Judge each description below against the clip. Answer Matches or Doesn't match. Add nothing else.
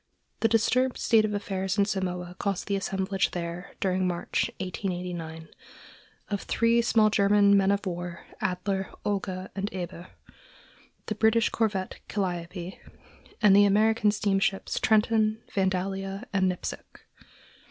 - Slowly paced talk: Matches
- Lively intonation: Doesn't match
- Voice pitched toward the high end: Matches